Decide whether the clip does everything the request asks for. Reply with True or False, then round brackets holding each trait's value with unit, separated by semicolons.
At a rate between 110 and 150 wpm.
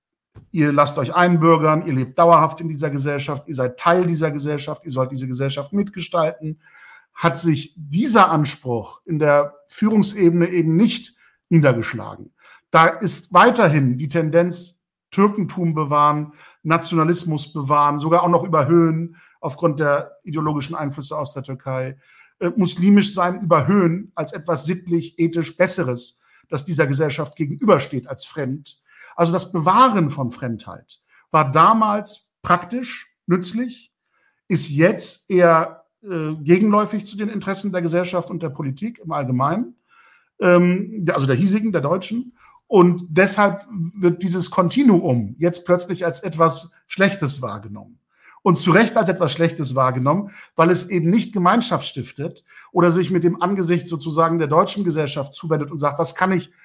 True (140 wpm)